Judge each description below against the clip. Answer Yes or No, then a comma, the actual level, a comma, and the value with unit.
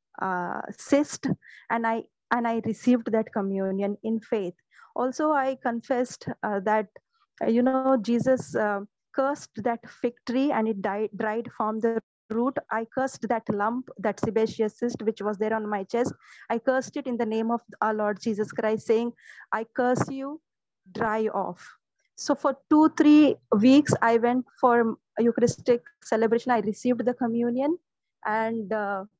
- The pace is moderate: Yes, average, 160 wpm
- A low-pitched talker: No, high, 230 Hz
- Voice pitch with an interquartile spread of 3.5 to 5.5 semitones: No, narrow, 2.6 semitones